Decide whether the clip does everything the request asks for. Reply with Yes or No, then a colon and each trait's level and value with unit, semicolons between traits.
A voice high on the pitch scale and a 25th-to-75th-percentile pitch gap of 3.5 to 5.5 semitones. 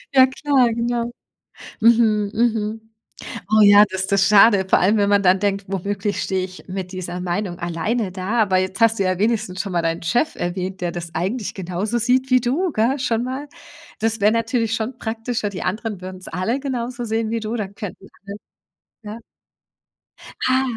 Yes: high, 210 Hz; average, 3.8 semitones